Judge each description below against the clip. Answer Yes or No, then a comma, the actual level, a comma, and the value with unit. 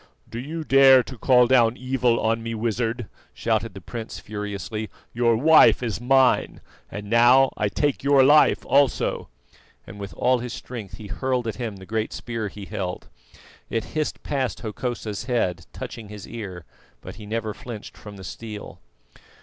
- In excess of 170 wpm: No, average, 165 wpm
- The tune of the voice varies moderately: Yes, average, 3.5 semitones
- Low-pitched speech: Yes, low, 115 Hz